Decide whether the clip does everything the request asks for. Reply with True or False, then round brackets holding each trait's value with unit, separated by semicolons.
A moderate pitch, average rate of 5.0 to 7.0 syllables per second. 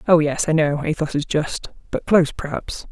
True (155 Hz; 5.2 syllables/s)